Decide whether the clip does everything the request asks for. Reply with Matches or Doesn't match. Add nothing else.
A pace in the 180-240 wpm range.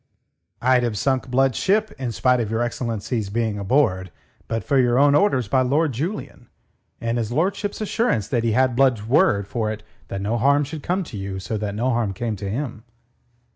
Matches